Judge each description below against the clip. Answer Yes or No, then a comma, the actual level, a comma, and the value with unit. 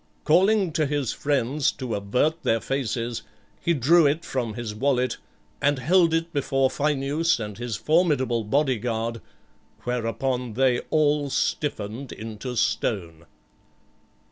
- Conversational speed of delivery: No, slow, 125 wpm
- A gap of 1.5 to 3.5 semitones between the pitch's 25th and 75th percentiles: No, average, 4.5 semitones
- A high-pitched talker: No, low, 130 Hz